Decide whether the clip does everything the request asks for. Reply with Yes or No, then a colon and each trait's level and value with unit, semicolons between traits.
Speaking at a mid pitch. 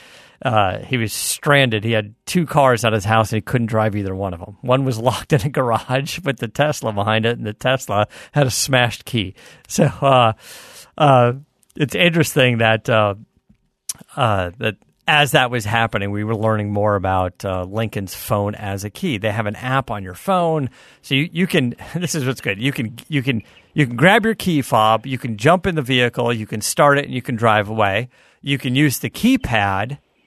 No: low, 120 Hz